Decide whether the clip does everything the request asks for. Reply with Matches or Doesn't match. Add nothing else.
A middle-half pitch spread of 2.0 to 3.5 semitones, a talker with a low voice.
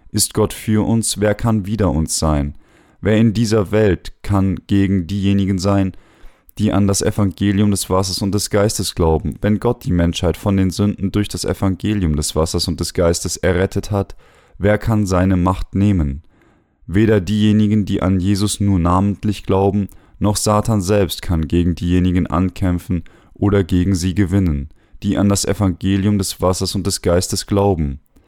Matches